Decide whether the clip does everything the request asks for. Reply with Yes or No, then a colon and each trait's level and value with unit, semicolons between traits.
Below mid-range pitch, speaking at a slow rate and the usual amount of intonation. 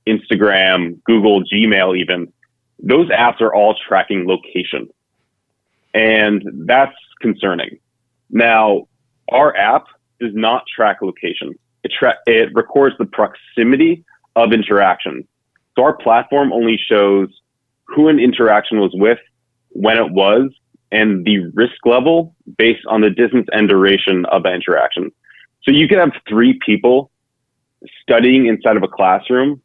Yes: low, 115 Hz; slow, 130 wpm; average, 3.3 semitones